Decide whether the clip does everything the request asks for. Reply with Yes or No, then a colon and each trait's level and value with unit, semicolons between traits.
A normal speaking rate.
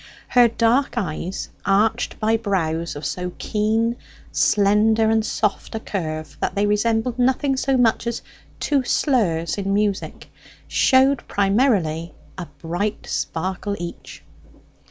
No: slow, 125 wpm